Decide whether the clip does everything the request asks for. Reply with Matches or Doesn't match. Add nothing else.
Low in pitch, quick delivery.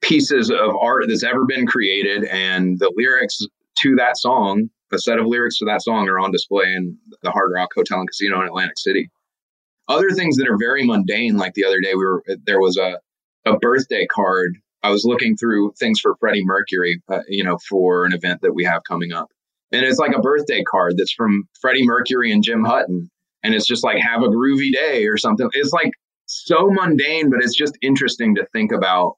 Matches